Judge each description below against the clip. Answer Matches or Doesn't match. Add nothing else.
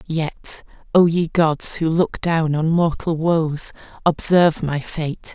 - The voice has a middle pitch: Matches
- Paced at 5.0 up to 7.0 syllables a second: Doesn't match